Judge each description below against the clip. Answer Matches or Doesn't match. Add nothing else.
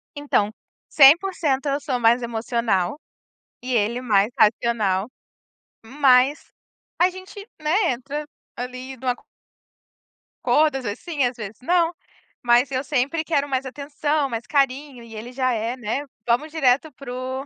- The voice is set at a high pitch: Matches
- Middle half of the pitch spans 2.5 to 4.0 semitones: Matches